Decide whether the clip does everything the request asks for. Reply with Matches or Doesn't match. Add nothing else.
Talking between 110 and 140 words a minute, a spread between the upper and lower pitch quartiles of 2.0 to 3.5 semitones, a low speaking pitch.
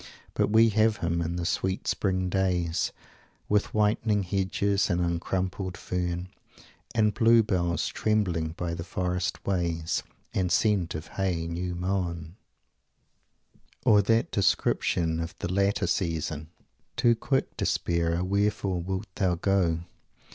Matches